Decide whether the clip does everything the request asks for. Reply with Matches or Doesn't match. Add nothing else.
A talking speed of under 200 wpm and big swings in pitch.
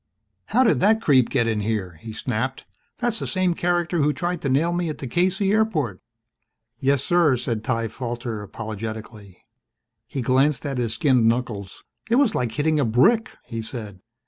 Matches